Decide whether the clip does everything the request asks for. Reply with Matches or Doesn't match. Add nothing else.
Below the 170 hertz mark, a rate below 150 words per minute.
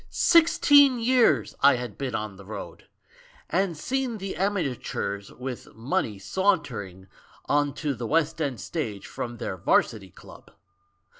Matches